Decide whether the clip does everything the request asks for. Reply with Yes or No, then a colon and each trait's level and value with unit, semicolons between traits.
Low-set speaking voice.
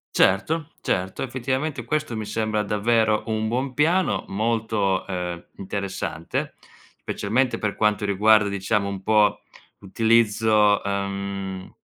Yes: low, 105 Hz